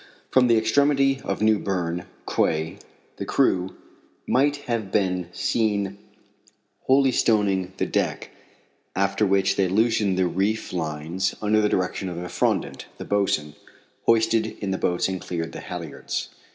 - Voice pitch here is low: Yes, low, 100 Hz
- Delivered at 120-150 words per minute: Yes, average, 140 wpm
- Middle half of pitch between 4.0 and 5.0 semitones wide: No, average, 3.3 semitones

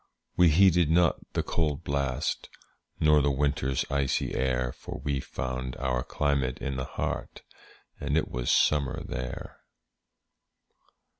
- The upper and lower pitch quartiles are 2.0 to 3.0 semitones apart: Yes, average, 2.7 semitones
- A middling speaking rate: No, slow, 130 wpm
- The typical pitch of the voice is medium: No, very low, 70 Hz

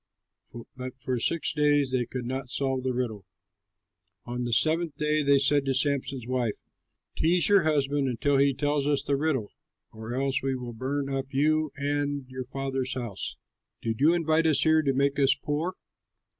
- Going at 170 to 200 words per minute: Yes, average, 175 wpm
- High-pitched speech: No, medium, 140 Hz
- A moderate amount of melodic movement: No, narrow, 2.3 semitones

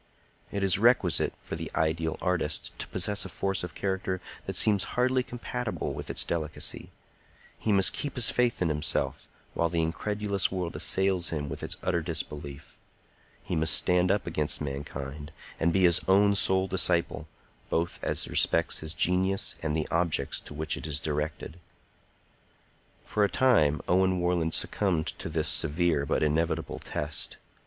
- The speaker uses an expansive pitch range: No, average, 3.7 semitones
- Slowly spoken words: No, average, 160 wpm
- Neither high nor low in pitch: No, very low, 85 Hz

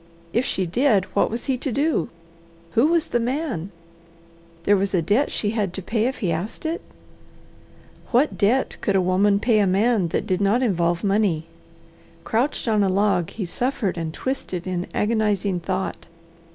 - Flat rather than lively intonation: No, average, 4.6 semitones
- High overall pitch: Yes, high, 205 Hz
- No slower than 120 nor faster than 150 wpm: No, average, 175 wpm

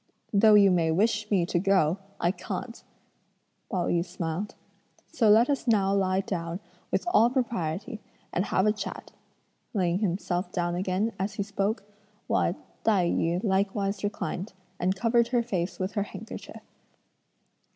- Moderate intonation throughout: Yes, average, 3.1 semitones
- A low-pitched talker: No, high, 195 Hz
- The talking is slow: No, average, 150 wpm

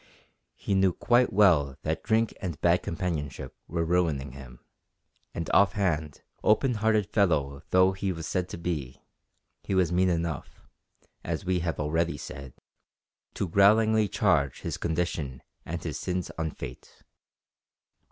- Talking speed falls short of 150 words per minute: Yes, average, 140 wpm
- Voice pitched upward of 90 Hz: No, very low, 85 Hz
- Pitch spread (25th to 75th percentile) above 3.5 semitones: Yes, average, 4.1 semitones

